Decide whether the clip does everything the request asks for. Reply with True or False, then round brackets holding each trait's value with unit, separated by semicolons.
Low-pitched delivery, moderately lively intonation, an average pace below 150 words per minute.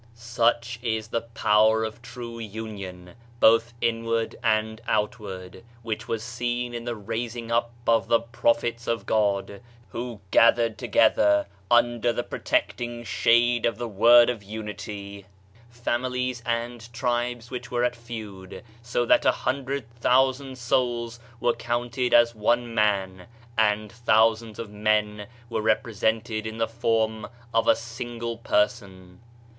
False (115 Hz; 1.8 semitones; 135 wpm)